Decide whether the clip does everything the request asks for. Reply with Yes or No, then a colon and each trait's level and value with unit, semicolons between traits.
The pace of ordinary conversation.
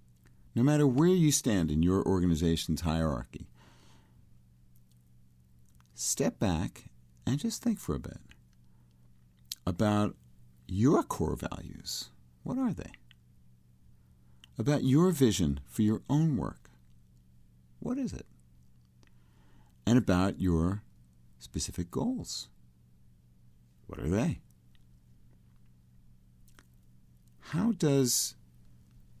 No: slow, 90 wpm